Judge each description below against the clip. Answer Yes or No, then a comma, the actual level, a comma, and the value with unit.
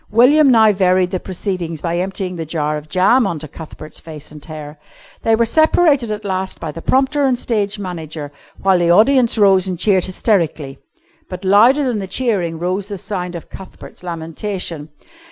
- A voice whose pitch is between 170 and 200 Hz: Yes, medium, 185 Hz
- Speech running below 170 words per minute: No, average, 180 wpm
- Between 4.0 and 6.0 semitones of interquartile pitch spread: Yes, average, 4.5 semitones